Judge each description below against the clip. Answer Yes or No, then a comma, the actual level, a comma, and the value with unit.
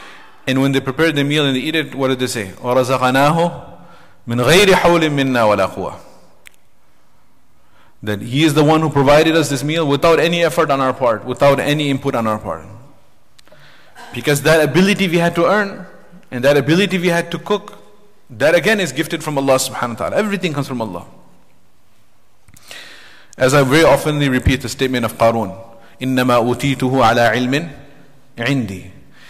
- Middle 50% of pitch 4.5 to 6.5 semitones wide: Yes, average, 4.8 semitones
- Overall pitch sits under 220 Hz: Yes, medium, 140 Hz